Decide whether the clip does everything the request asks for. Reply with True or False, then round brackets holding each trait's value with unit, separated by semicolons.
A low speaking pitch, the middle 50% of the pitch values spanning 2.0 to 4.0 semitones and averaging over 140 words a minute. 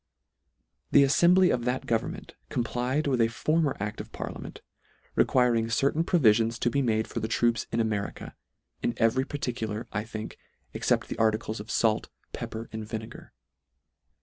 True (115 Hz; 2.8 semitones; 160 wpm)